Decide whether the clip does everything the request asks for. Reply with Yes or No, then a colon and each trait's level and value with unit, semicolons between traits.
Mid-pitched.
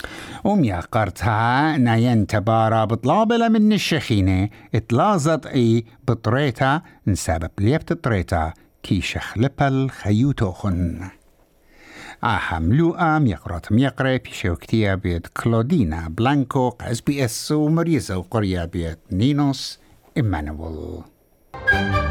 No: low, 115 Hz